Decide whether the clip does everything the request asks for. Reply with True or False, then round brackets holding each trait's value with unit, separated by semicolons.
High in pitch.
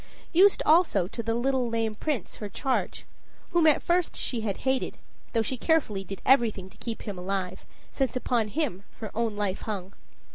True (230 Hz)